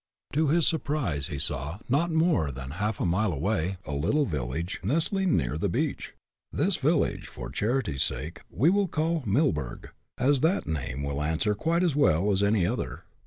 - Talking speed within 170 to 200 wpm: Yes, average, 175 wpm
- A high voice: No, low, 100 Hz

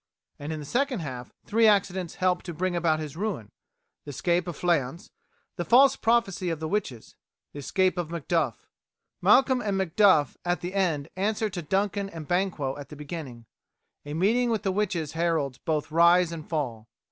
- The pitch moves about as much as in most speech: Yes, average, 4.4 semitones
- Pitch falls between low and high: Yes, medium, 175 Hz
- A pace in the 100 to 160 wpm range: No, average, 180 wpm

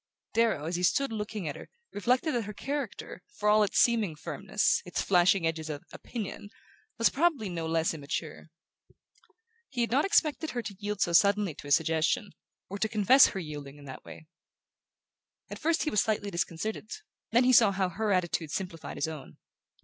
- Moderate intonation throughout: No, wide, 5.7 semitones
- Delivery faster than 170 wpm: Yes, average, 185 wpm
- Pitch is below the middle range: No, high, 200 Hz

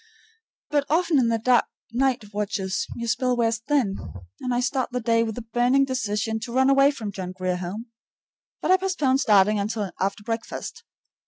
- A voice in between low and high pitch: No, high, 235 Hz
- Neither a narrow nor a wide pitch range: Yes, average, 4.0 semitones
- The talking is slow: No, average, 180 wpm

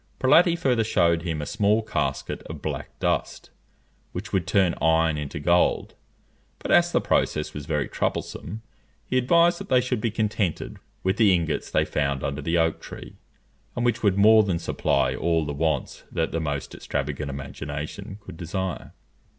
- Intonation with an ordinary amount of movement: No, wide, 6.2 semitones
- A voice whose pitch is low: Yes, very low, 85 Hz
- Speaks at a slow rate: No, average, 170 wpm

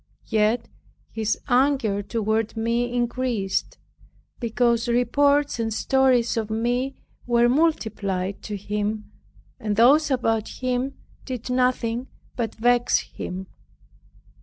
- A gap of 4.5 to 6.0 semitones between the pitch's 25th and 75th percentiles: No, narrow, 2.5 semitones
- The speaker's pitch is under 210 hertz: No, high, 235 Hz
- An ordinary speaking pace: No, slow, 105 wpm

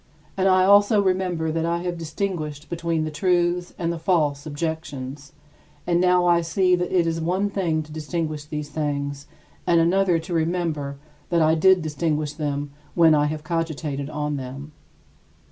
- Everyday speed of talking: Yes, average, 165 wpm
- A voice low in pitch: No, medium, 165 Hz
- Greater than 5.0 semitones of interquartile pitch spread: No, average, 2.8 semitones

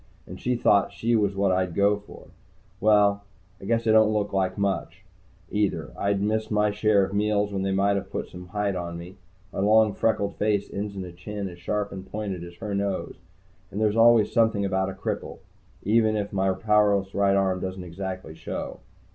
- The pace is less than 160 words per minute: No, fast, 205 wpm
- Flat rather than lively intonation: Yes, narrow, 1.8 semitones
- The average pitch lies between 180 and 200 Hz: No, low, 100 Hz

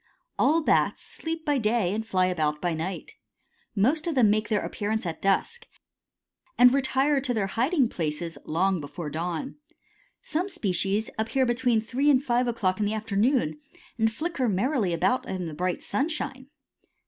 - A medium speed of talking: Yes, average, 160 wpm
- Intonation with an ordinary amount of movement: No, wide, 6.3 semitones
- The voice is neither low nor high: No, high, 220 Hz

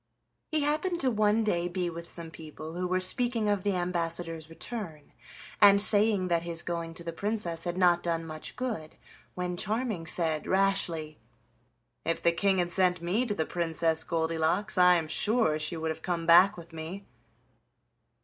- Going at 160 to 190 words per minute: Yes, average, 175 wpm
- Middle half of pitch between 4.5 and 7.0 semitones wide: No, average, 3.5 semitones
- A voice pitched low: No, medium, 175 Hz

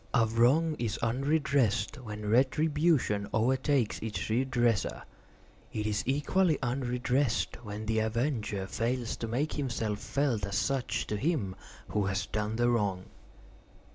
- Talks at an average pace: No, slow, 130 wpm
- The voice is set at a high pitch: No, low, 120 Hz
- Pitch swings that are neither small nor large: Yes, average, 4.3 semitones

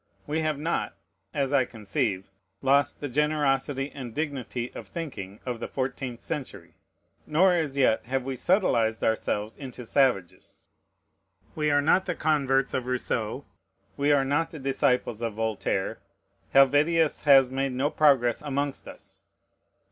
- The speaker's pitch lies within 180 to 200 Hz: No, low, 135 Hz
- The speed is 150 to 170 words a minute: No, average, 140 wpm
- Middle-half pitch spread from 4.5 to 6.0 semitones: No, average, 3.4 semitones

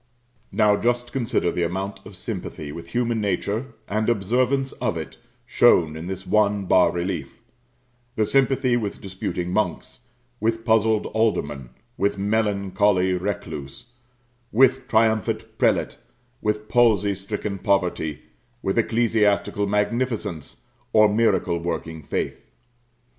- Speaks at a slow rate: Yes, slow, 115 wpm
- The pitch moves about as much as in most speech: Yes, average, 3.7 semitones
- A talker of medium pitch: No, low, 105 Hz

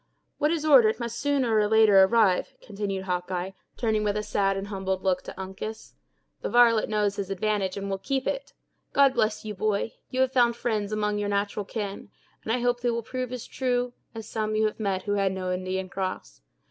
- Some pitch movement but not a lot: Yes, average, 3.3 semitones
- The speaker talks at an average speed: No, fast, 210 wpm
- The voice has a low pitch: No, high, 210 Hz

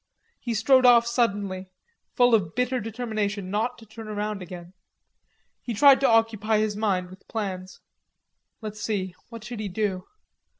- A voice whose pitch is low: No, high, 215 Hz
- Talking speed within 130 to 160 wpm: Yes, average, 155 wpm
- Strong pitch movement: No, average, 2.8 semitones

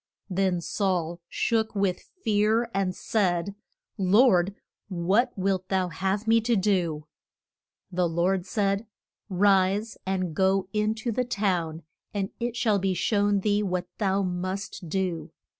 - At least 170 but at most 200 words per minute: No, slow, 135 wpm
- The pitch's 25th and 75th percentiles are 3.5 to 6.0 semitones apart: No, narrow, 2.4 semitones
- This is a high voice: Yes, high, 195 Hz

